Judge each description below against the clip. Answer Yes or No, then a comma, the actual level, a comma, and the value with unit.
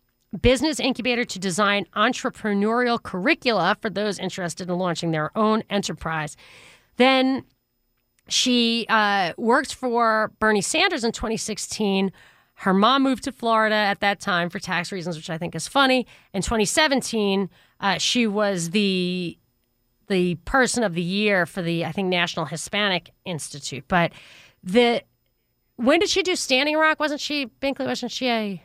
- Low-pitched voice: No, high, 210 Hz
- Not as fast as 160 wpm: Yes, average, 150 wpm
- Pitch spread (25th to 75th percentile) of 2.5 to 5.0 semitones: No, wide, 5.6 semitones